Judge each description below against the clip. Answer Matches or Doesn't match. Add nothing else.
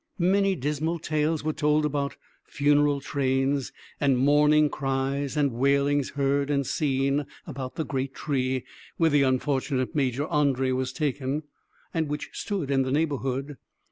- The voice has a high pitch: Doesn't match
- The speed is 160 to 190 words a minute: Doesn't match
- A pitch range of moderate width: Doesn't match